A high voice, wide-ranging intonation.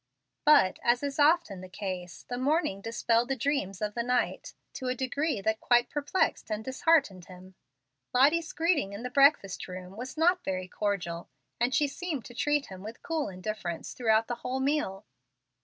Yes: high, 240 Hz; wide, 6.5 semitones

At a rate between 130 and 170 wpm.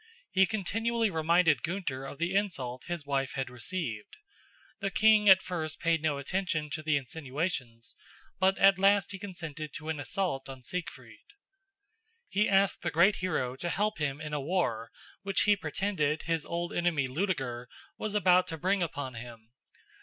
Yes: average, 165 wpm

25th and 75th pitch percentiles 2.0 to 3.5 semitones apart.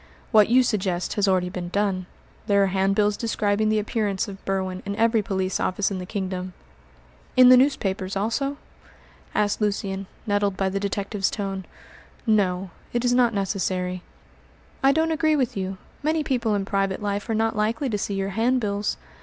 Yes: average, 2.8 semitones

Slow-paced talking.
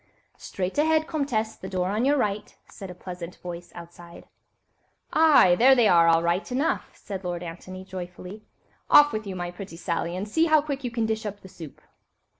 No: average, 195 wpm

